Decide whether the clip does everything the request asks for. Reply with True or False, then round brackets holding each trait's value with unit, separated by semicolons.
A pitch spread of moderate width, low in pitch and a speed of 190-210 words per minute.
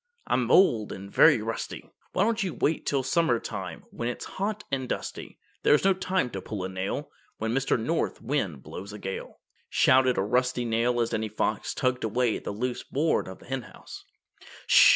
True (4.8 semitones; 125 Hz; 195 wpm)